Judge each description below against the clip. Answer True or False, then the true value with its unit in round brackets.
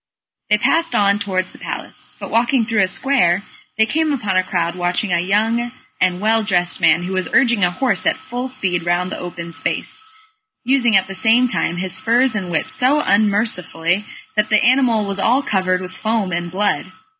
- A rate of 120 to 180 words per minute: False (195 wpm)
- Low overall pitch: False (200 Hz)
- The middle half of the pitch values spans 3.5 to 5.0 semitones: True (4.5 semitones)